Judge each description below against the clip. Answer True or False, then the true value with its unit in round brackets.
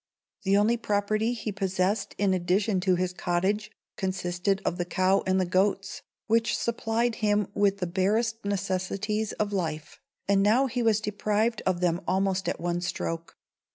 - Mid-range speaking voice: False (195 Hz)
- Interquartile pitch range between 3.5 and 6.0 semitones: False (2.5 semitones)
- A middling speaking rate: True (160 wpm)